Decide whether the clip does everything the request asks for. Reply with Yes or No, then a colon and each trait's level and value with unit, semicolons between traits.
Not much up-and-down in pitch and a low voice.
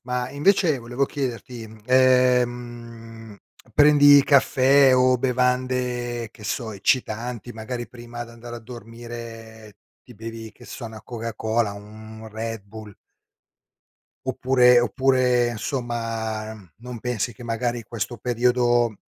Yes: narrow, 2.0 semitones; low, 120 Hz